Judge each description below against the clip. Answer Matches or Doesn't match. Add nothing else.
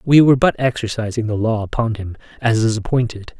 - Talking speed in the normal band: Matches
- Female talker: Doesn't match